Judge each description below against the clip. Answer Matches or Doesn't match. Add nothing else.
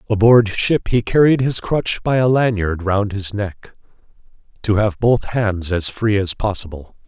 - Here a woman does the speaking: Doesn't match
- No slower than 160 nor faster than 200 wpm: Matches